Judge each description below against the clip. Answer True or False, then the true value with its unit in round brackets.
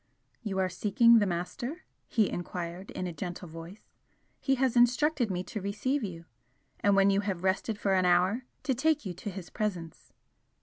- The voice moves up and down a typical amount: True (4.6 semitones)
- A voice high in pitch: True (195 Hz)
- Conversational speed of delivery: True (180 wpm)